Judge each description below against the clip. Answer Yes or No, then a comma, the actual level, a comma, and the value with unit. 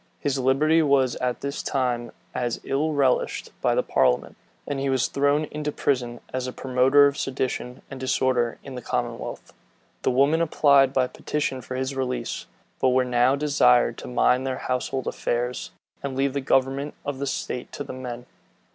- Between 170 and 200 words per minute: Yes, average, 175 wpm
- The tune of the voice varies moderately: No, narrow, 1.8 semitones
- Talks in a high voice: No, low, 130 Hz